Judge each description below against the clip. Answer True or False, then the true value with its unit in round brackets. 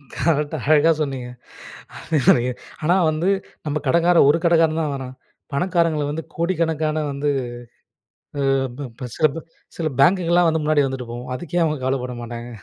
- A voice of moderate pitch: True (155 Hz)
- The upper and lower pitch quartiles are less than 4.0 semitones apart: True (3.3 semitones)